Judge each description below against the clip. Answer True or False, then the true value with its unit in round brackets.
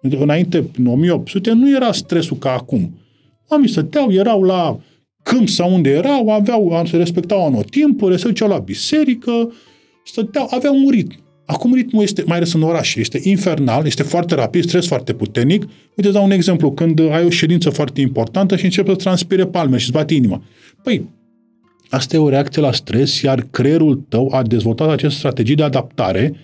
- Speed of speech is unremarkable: False (180 wpm)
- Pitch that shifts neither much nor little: False (6.3 semitones)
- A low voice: False (170 Hz)